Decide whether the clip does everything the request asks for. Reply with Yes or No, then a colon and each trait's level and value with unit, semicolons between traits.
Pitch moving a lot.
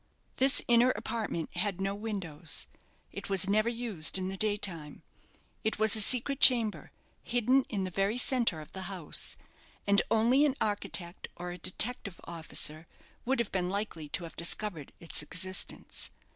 No: average, 4.5 semitones